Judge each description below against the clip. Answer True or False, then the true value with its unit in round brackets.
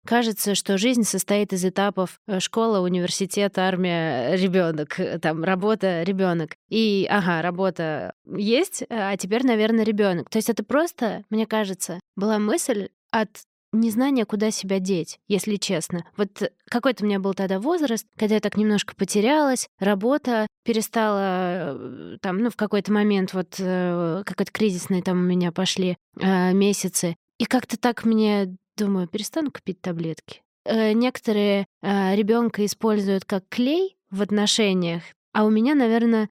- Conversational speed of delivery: True (140 wpm)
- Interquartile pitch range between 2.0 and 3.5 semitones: True (2.9 semitones)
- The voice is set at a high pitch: True (205 Hz)